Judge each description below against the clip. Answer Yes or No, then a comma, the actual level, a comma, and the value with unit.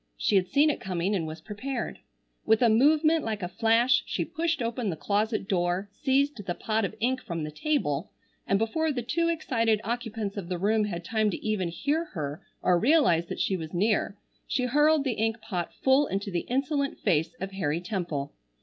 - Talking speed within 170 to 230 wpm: Yes, average, 200 wpm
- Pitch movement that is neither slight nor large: No, wide, 6.4 semitones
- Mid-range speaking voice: No, high, 215 Hz